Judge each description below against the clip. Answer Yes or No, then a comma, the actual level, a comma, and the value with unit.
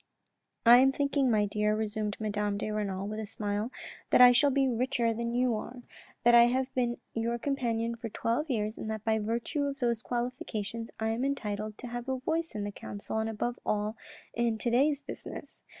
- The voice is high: Yes, high, 230 Hz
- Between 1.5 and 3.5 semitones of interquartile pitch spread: Yes, average, 2.8 semitones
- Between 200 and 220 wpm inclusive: Yes, fast, 205 wpm